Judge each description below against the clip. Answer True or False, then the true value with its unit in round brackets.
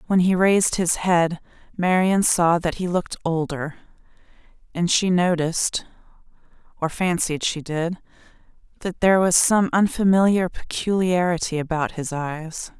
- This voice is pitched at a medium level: True (175 Hz)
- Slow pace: True (115 wpm)